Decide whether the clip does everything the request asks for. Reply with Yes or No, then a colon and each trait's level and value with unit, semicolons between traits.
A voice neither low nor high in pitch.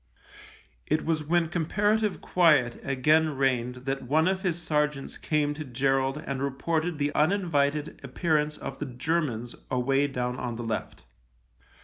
Yes: medium, 145 Hz